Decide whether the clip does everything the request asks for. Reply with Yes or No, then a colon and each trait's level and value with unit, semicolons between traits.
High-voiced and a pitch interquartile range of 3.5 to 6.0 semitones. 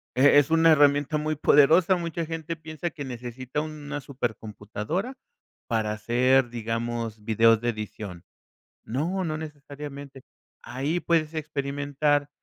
No: medium, 140 Hz; average, 4.7 semitones